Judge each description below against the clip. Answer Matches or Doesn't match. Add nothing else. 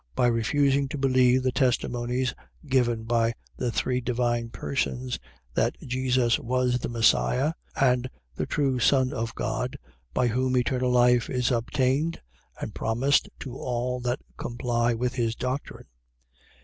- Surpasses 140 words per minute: Doesn't match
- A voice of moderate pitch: Doesn't match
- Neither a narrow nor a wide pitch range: Doesn't match